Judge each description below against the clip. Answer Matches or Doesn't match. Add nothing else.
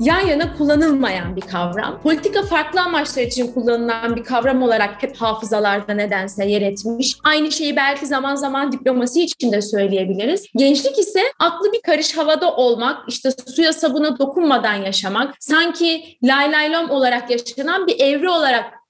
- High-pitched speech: Matches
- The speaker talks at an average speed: Doesn't match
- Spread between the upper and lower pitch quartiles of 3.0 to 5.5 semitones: Matches